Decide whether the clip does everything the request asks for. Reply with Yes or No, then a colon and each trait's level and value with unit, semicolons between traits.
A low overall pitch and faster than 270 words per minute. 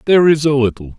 No: low, 130 Hz; fast, 245 wpm